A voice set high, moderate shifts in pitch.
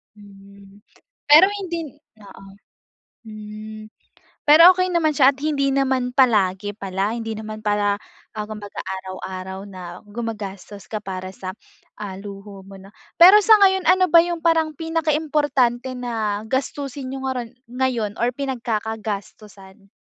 No: high, 220 Hz; wide, 5.7 semitones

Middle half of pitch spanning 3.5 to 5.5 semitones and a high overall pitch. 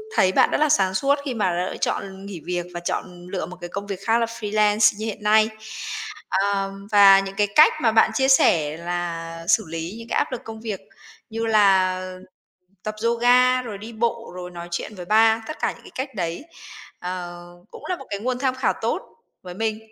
Yes: average, 3.9 semitones; high, 205 Hz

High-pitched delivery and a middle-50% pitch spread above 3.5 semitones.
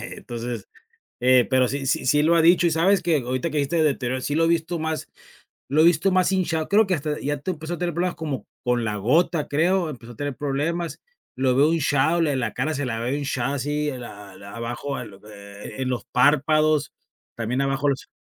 No: medium, 145 Hz; average, 4.2 semitones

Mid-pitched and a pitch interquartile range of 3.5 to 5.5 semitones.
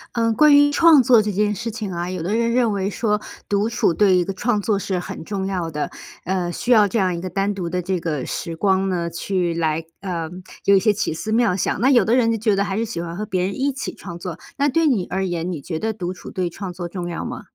No: high, 195 Hz; average, 4.0 semitones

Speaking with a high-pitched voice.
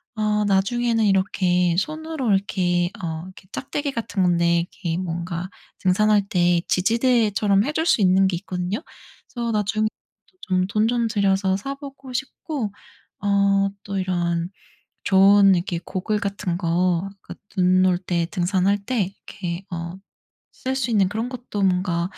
Yes: high, 195 Hz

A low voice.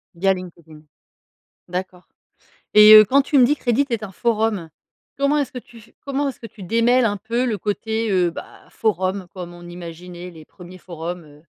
No: high, 200 Hz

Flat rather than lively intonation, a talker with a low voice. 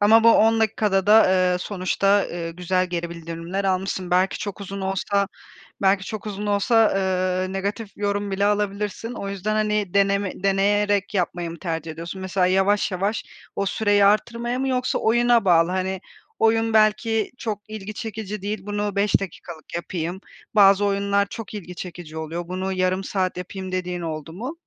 No: narrow, 2.2 semitones; high, 195 Hz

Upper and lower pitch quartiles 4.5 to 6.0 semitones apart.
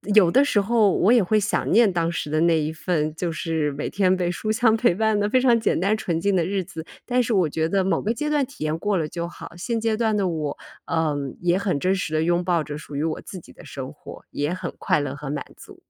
Yes: average, 5.0 semitones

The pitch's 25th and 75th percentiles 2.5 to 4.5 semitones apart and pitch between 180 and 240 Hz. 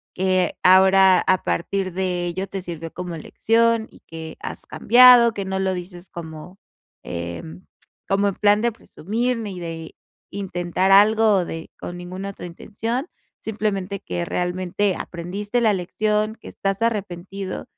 Yes: average, 2.9 semitones; high, 190 Hz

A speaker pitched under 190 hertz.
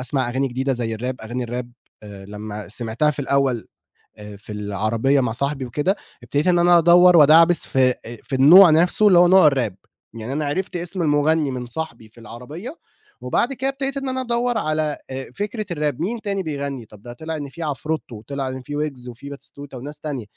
Yes: medium, 140 Hz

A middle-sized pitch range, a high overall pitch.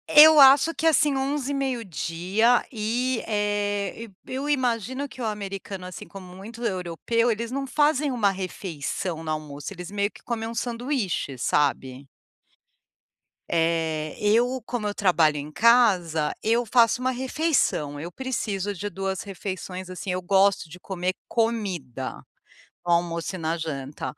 No: wide, 5.9 semitones; high, 205 Hz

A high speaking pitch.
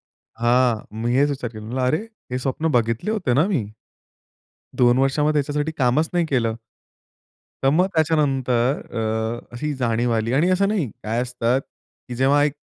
No: low, 130 Hz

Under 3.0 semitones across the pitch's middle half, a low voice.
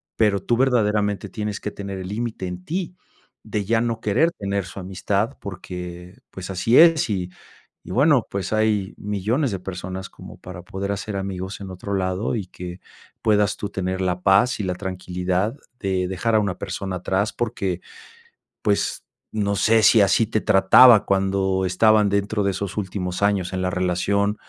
Yes: narrow, 2.5 semitones; low, 100 Hz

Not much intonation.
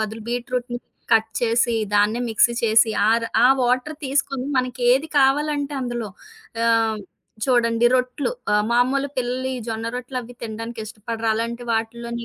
Yes: narrow, 1.9 semitones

